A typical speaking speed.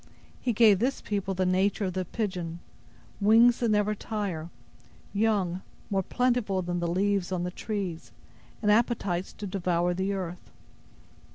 Yes: average, 150 wpm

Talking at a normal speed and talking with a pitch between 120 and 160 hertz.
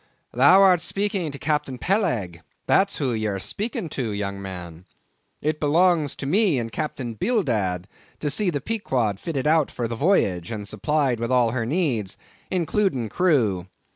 Yes: average, 160 wpm; low, 135 Hz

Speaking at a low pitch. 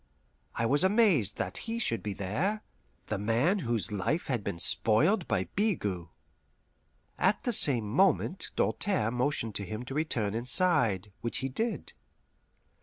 Yes: low, 125 Hz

